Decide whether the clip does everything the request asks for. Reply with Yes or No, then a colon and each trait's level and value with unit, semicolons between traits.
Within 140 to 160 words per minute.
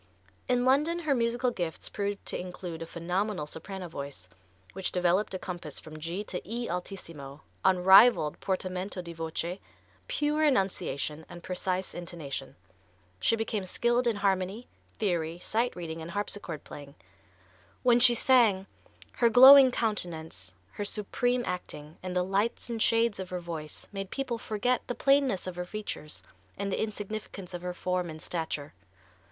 Yes: average, 150 wpm